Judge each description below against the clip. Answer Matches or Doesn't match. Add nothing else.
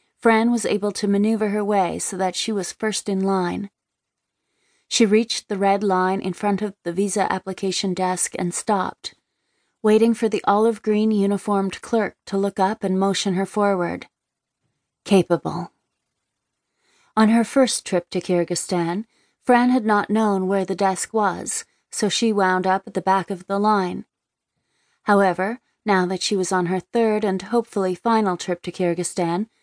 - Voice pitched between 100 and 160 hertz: Doesn't match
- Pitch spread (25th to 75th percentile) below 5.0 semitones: Matches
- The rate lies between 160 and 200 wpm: Matches